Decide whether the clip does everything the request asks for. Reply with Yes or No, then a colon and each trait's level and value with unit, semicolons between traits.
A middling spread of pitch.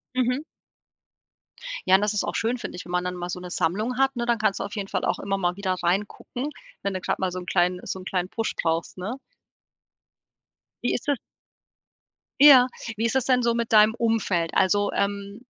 Yes: average, 4.4 semitones